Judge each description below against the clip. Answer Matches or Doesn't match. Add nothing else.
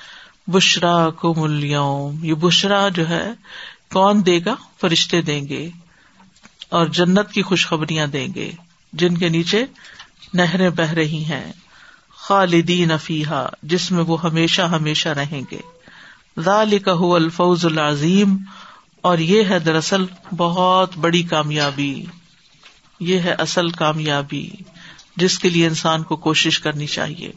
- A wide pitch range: Doesn't match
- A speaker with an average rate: Matches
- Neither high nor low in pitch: Matches